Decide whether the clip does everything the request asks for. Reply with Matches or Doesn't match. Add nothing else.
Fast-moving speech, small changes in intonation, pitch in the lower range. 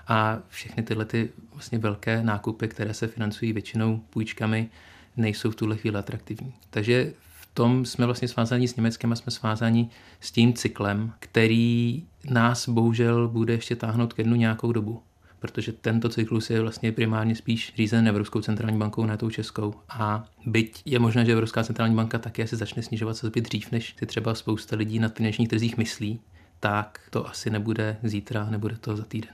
Matches